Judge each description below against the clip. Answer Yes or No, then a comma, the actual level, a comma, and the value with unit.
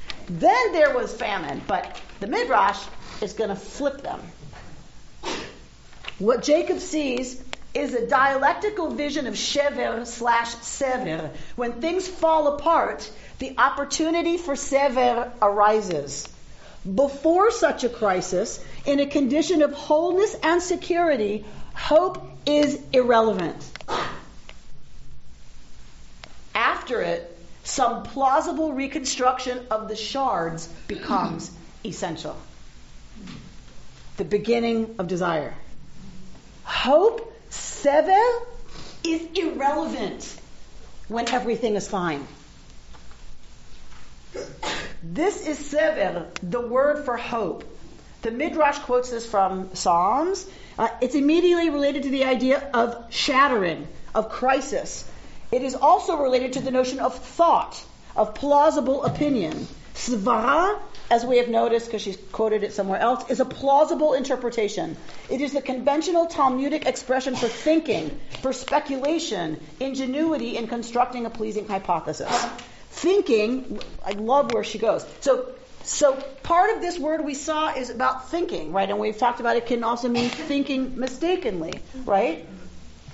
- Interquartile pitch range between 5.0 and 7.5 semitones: Yes, wide, 5.4 semitones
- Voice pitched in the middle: No, very high, 255 Hz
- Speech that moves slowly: Yes, slow, 120 wpm